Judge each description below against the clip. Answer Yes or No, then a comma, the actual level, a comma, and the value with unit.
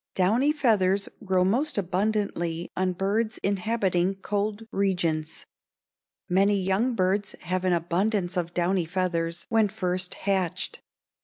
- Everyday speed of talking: No, slow, 115 wpm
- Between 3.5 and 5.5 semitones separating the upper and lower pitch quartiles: No, narrow, 2.5 semitones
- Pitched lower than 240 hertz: Yes, high, 190 Hz